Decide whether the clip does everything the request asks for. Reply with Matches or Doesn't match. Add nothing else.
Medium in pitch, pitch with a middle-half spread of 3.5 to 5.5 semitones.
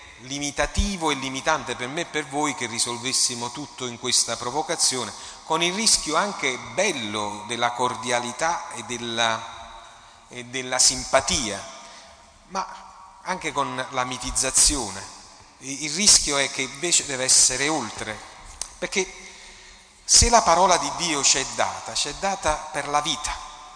Doesn't match